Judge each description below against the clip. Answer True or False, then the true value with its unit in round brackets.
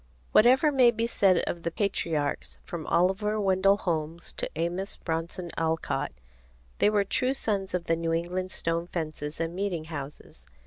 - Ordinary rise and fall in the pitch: True (3.4 semitones)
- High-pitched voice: False (175 Hz)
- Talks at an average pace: True (160 wpm)